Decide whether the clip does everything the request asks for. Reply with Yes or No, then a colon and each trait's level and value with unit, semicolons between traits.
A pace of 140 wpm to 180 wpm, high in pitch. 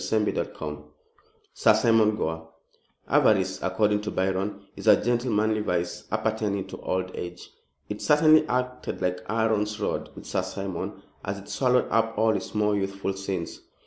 No: average, 150 wpm; low, 105 Hz